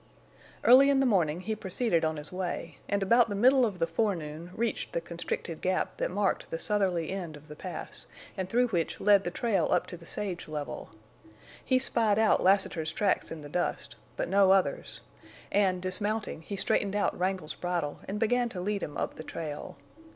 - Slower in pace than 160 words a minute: No, average, 195 wpm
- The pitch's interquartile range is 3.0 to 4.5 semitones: Yes, average, 3.9 semitones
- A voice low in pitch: No, high, 190 Hz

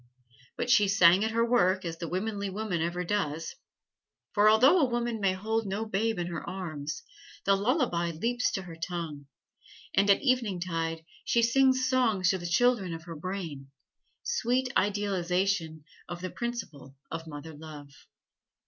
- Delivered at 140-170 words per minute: Yes, average, 155 wpm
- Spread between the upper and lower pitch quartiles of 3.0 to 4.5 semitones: No, average, 5.2 semitones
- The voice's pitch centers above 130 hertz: Yes, high, 190 Hz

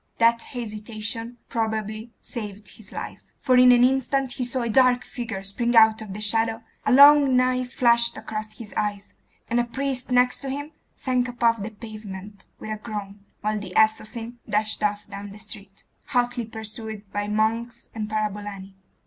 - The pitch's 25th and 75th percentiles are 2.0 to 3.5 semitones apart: Yes, narrow, 2.5 semitones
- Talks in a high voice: Yes, high, 225 Hz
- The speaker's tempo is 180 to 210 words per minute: No, average, 170 wpm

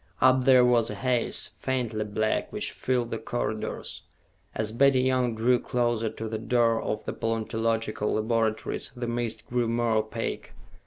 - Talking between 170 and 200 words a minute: No, average, 155 wpm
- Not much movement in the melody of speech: Yes, narrow, 1.9 semitones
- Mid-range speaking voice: No, low, 115 Hz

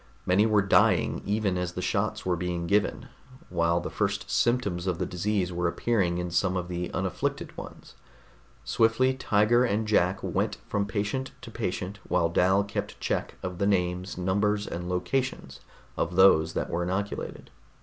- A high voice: No, very low, 95 Hz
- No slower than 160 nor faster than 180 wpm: Yes, average, 165 wpm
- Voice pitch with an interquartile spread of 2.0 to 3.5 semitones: Yes, average, 2.9 semitones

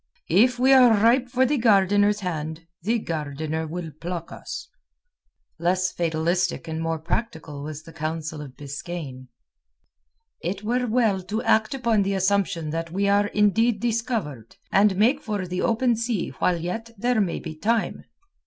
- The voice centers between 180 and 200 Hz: Yes, high, 190 Hz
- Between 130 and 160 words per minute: Yes, average, 155 wpm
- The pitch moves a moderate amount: No, wide, 5.7 semitones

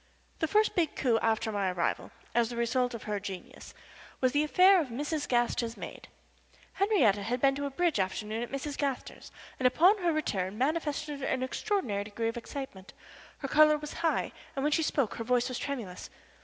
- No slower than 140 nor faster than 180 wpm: No, average, 195 wpm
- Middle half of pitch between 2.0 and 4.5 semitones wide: No, average, 5.0 semitones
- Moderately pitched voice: No, very high, 260 Hz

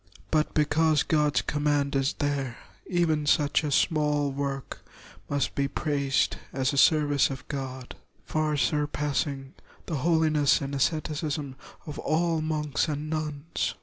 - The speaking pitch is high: No, medium, 145 Hz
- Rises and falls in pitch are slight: Yes, narrow, 1.8 semitones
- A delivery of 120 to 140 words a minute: Yes, slow, 135 wpm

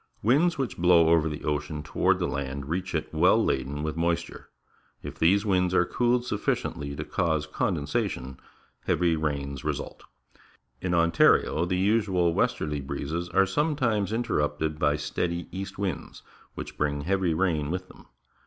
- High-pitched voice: No, very low, 85 Hz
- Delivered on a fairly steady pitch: No, average, 4.2 semitones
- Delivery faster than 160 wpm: No, average, 145 wpm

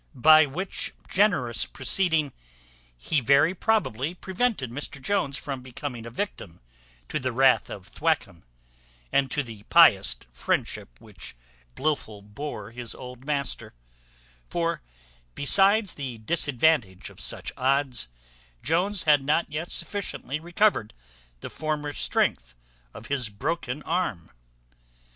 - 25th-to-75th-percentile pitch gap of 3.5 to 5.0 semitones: No, wide, 5.6 semitones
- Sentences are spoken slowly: Yes, slow, 120 wpm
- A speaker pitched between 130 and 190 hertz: Yes, medium, 140 Hz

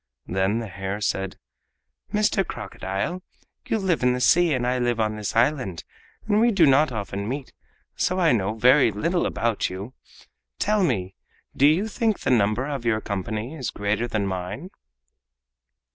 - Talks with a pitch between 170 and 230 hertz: No, low, 120 Hz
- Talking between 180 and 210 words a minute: No, average, 165 wpm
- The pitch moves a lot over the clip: Yes, wide, 7.7 semitones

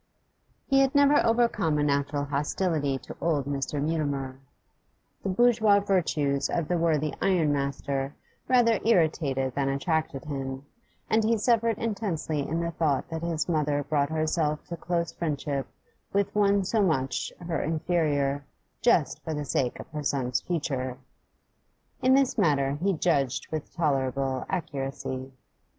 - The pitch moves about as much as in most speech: Yes, average, 4.7 semitones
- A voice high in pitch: No, medium, 155 Hz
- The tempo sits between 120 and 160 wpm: Yes, average, 140 wpm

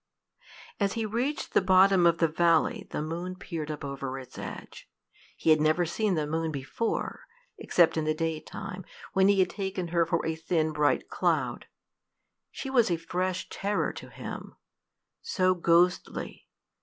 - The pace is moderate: Yes, average, 160 wpm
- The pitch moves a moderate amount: Yes, average, 3.3 semitones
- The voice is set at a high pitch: No, medium, 170 Hz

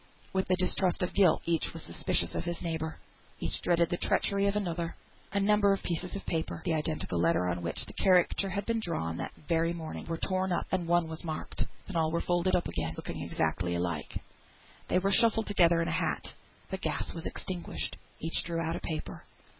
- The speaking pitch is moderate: Yes, medium, 170 Hz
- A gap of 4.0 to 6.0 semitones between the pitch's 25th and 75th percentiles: No, average, 2.8 semitones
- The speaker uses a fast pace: Yes, fast, 210 wpm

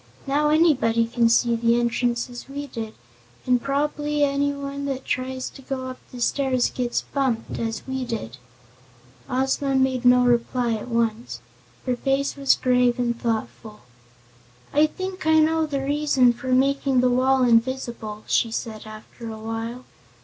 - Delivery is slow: No, average, 155 wpm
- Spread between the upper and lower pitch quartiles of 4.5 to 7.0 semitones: No, average, 2.9 semitones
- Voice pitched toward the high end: Yes, very high, 255 Hz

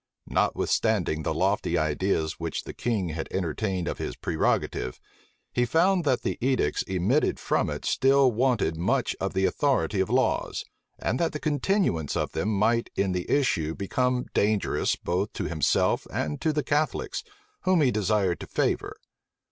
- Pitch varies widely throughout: Yes, wide, 7.0 semitones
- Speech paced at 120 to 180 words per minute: Yes, average, 160 wpm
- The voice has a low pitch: Yes, low, 105 Hz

